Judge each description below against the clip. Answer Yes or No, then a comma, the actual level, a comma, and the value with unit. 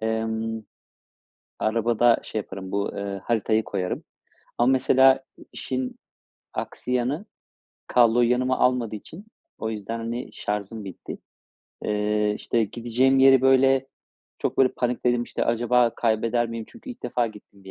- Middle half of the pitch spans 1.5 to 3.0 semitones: Yes, narrow, 2.6 semitones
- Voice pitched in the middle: No, low, 115 Hz